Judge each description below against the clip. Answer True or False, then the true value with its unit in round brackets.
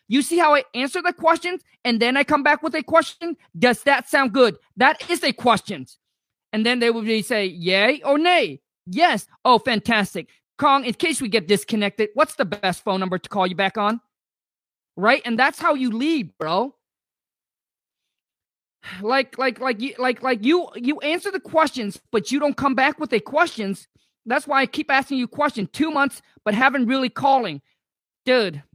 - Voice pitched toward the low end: False (260 Hz)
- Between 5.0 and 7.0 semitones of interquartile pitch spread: True (5.3 semitones)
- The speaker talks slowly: False (190 wpm)